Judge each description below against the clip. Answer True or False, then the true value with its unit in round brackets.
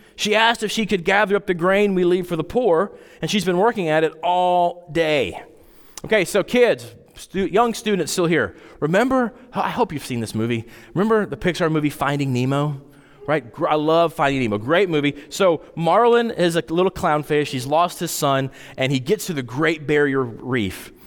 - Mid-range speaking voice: True (165 Hz)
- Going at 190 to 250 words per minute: True (195 wpm)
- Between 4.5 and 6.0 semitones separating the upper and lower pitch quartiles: True (5.5 semitones)